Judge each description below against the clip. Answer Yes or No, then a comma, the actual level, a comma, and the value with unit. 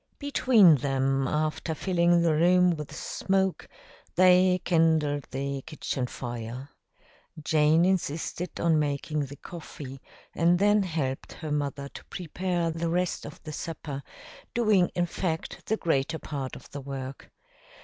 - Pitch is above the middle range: No, medium, 160 Hz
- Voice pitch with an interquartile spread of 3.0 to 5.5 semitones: Yes, average, 4.0 semitones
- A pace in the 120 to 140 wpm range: Yes, slow, 135 wpm